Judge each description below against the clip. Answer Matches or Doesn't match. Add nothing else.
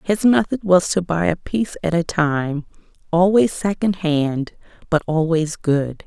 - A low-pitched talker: Doesn't match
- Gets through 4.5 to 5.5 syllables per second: Doesn't match